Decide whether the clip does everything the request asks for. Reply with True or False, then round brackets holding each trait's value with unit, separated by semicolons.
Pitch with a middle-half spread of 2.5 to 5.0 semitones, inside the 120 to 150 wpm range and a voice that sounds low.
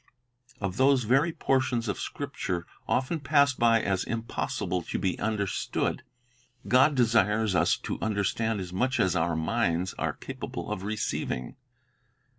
False (5.5 semitones; 140 wpm; 110 Hz)